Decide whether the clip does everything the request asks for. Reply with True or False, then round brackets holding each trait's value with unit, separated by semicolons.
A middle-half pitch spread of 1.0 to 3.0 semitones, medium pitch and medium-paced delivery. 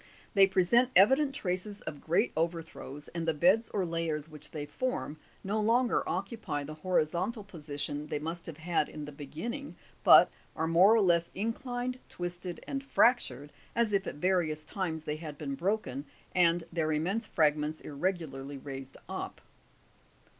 False (5.1 semitones; 170 Hz; 160 wpm)